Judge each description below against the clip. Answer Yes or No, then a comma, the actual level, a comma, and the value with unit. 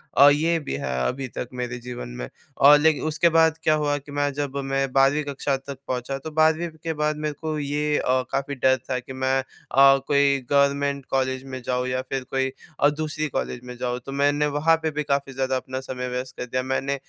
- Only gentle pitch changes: Yes, narrow, 2.2 semitones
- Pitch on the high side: No, medium, 140 Hz